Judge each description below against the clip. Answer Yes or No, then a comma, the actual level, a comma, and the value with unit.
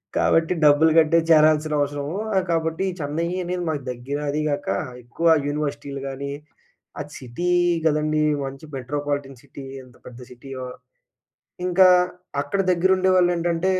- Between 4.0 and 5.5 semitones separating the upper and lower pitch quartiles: No, average, 3.1 semitones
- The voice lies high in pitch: No, medium, 150 Hz